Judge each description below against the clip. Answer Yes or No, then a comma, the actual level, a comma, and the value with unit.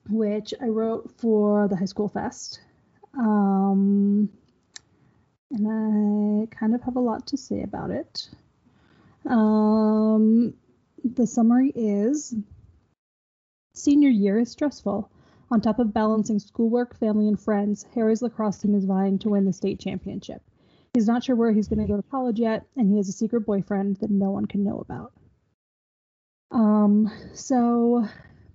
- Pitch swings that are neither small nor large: No, narrow, 2.3 semitones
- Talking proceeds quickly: No, average, 150 wpm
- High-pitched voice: Yes, high, 215 Hz